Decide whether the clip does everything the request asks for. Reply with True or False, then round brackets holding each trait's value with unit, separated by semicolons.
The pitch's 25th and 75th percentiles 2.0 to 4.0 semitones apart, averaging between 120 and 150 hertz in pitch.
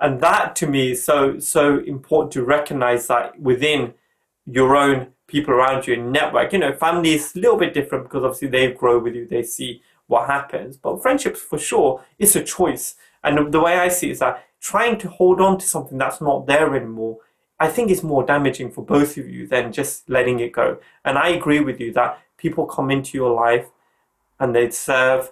True (3.7 semitones; 140 Hz)